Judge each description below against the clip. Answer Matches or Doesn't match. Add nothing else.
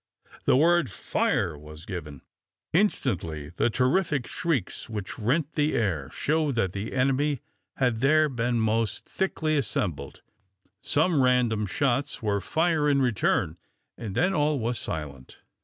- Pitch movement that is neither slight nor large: Doesn't match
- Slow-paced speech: Matches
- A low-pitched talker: Matches